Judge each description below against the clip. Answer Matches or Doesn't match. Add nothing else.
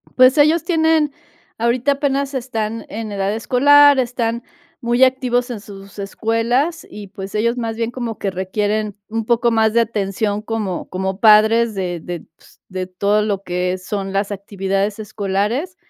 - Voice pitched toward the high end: Matches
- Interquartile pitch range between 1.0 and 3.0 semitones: Doesn't match